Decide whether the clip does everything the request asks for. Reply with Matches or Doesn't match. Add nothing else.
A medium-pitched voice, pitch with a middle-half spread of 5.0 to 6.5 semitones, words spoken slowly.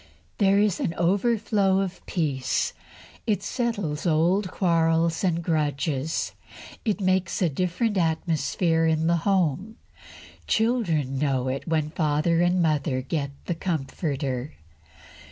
Doesn't match